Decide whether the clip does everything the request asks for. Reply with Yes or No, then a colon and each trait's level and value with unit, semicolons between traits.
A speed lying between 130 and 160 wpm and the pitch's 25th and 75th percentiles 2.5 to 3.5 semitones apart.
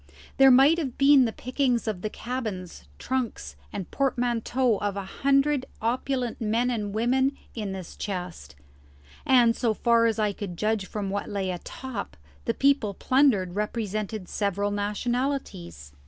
No: average, 145 wpm; average, 4.2 semitones